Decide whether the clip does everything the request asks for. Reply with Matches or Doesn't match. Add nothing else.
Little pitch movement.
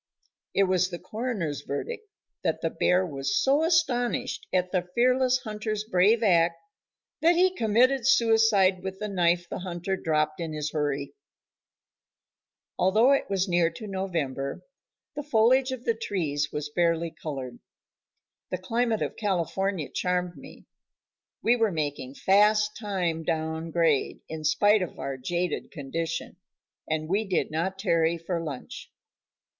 Doesn't match